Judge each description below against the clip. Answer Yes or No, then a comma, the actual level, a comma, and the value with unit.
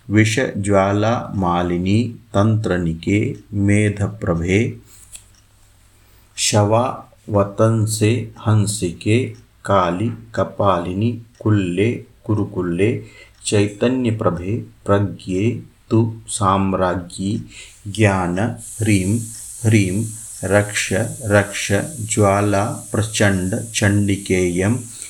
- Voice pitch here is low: Yes, low, 105 Hz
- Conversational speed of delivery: No, slow, 50 wpm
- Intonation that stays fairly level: Yes, narrow, 2.3 semitones